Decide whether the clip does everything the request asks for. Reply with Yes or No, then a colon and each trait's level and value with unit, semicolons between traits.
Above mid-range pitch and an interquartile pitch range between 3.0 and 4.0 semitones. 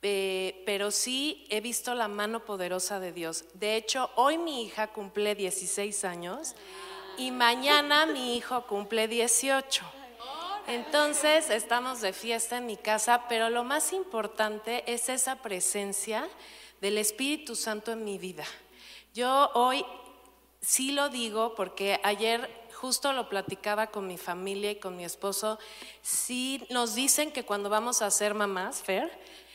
Yes: high, 225 Hz; average, 3.7 semitones